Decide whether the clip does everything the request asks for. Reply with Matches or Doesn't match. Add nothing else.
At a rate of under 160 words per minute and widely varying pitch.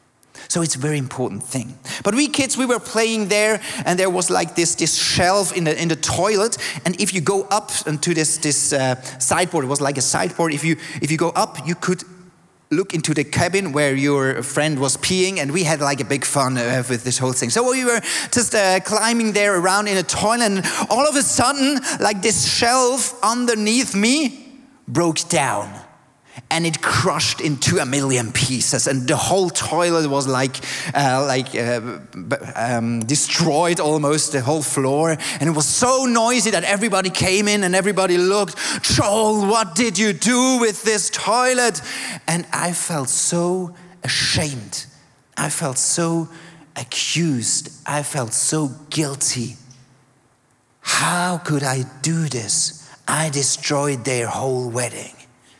Doesn't match